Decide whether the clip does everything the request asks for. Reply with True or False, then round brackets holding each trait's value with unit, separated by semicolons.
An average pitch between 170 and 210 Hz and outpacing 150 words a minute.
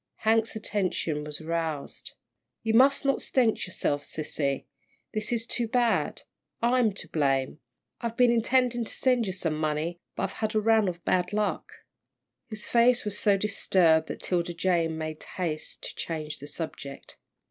True (190 Hz; 160 wpm)